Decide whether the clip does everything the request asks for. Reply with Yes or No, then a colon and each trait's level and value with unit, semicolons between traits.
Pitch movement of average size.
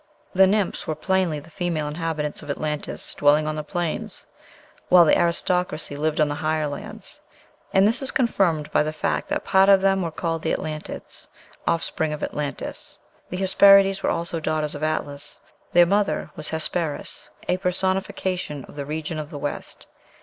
Yes: average, 3.5 semitones